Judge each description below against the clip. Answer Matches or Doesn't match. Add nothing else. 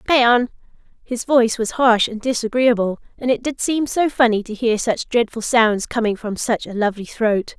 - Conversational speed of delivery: Matches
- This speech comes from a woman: Matches